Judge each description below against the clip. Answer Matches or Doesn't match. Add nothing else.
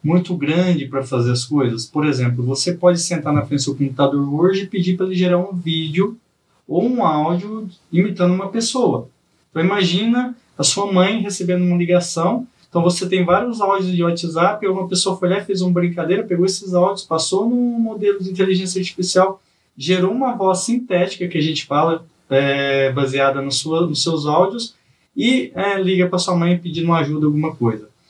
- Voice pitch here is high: Doesn't match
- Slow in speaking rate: Doesn't match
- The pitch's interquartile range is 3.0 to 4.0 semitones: Matches